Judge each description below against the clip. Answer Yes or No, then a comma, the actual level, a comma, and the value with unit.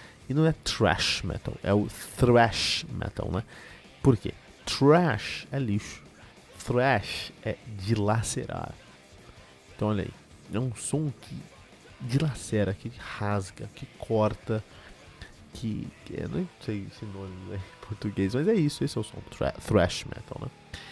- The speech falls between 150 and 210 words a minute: No, average, 140 wpm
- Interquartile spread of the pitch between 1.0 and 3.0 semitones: No, average, 4.6 semitones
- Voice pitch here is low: Yes, low, 105 Hz